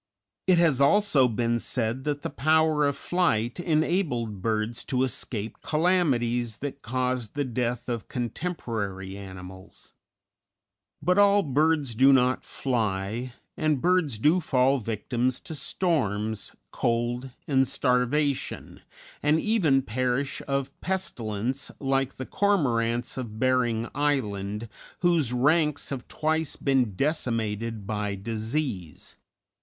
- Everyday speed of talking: No, slow, 115 wpm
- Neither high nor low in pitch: No, low, 130 Hz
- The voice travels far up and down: No, average, 4.6 semitones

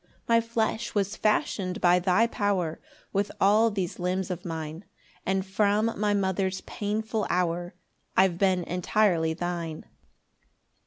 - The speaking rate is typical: No, slow, 130 wpm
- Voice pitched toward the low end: No, high, 190 Hz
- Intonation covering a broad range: No, average, 2.9 semitones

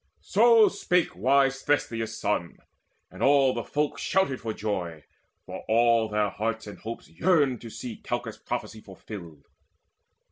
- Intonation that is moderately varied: Yes, average, 4.9 semitones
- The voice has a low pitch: Yes, low, 115 Hz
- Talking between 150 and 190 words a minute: No, average, 140 wpm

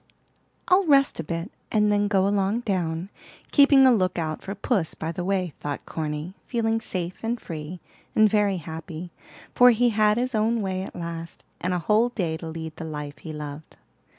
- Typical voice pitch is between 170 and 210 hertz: Yes, medium, 185 Hz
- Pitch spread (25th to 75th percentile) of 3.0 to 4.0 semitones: No, average, 5.1 semitones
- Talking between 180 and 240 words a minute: Yes, average, 190 wpm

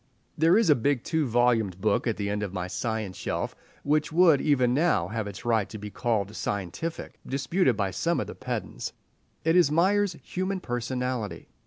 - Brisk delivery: No, average, 185 wpm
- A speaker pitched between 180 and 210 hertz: No, low, 125 Hz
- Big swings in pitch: Yes, wide, 7.4 semitones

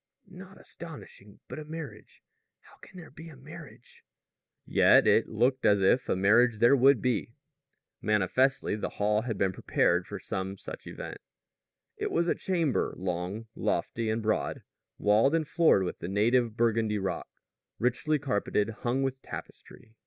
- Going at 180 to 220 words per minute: No, average, 155 wpm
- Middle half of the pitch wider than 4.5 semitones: Yes, average, 5.2 semitones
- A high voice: No, low, 120 Hz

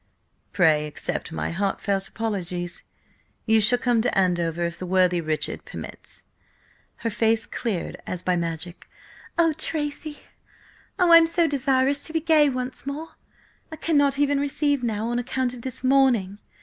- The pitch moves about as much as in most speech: No, wide, 7.7 semitones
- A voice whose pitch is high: Yes, high, 240 Hz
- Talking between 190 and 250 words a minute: No, average, 155 wpm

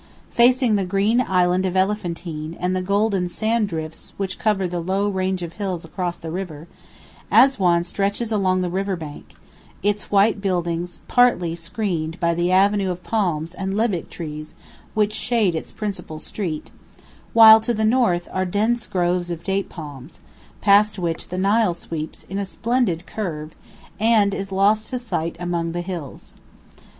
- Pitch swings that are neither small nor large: Yes, average, 3.4 semitones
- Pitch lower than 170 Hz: No, medium, 185 Hz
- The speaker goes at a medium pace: Yes, average, 160 wpm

